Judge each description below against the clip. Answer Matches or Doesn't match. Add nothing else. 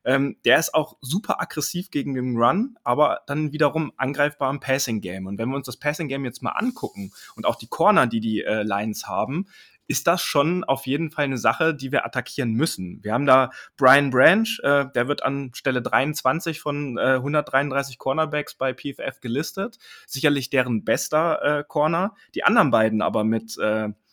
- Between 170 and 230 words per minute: Matches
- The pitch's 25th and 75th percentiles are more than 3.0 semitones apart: Matches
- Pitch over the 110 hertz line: Matches